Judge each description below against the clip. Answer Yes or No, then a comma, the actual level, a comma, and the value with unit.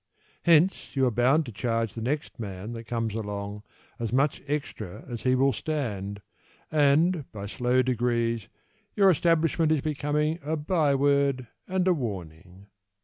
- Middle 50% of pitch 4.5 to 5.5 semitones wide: Yes, average, 5.2 semitones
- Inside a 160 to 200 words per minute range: No, average, 150 wpm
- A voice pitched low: Yes, low, 130 Hz